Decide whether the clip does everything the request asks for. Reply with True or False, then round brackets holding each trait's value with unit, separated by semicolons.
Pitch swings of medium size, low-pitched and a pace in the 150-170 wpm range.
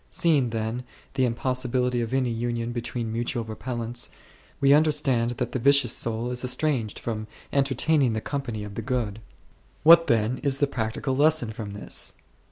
True (3.1 semitones; 120 Hz; 165 wpm)